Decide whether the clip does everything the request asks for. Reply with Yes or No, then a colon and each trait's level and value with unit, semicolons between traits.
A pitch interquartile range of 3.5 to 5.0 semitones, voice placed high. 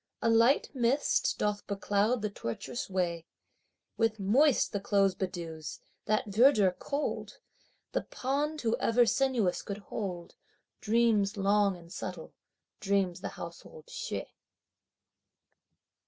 Yes: average, 3.8 semitones; high, 205 Hz